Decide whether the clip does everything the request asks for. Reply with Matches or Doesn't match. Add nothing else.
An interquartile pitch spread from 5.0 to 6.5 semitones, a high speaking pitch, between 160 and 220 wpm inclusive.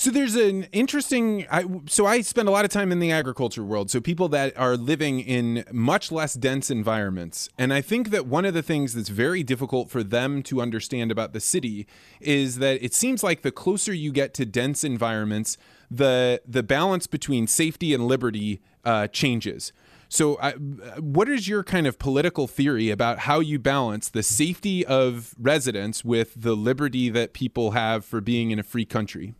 Doesn't match